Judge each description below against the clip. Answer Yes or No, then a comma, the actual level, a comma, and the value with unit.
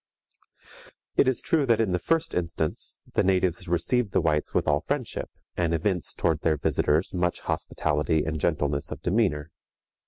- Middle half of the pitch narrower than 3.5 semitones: No, average, 4.3 semitones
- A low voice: Yes, very low, 85 Hz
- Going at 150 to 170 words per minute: Yes, average, 160 wpm